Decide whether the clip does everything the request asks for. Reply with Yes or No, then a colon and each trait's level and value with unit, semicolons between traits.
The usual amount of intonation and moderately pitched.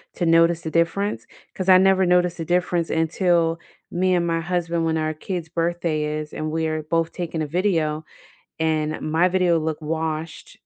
No: narrow, 1.8 semitones; medium, 165 Hz